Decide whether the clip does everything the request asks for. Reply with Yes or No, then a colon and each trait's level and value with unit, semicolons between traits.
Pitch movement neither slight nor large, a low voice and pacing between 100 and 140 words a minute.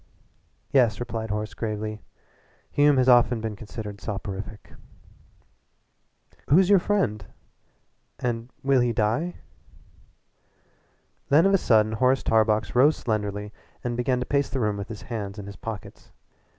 Yes: average, 3.5 semitones; low, 115 Hz; slow, 135 wpm